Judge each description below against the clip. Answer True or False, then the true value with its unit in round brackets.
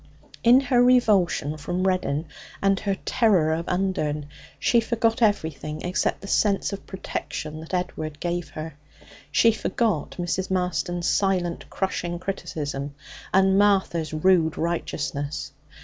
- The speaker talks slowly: True (125 wpm)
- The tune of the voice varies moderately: True (3.8 semitones)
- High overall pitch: False (180 Hz)